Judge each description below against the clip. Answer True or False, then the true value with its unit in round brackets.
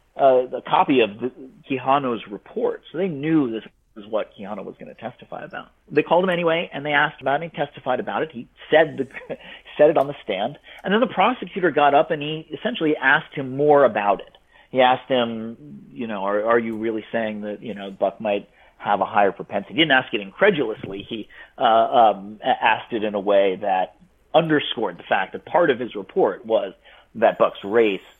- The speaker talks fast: True (210 wpm)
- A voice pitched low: True (130 Hz)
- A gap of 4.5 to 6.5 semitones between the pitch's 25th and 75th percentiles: True (5.6 semitones)